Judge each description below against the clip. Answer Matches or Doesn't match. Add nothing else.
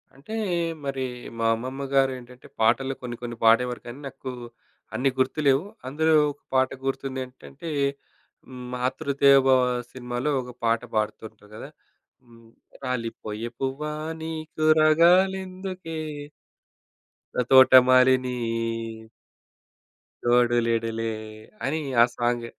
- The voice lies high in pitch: Doesn't match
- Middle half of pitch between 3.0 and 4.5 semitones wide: Doesn't match